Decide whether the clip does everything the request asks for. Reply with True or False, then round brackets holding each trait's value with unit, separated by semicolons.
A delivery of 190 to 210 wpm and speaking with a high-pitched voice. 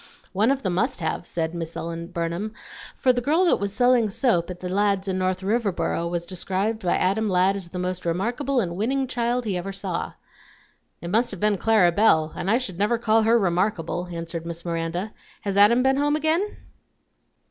True (200 wpm; 195 Hz)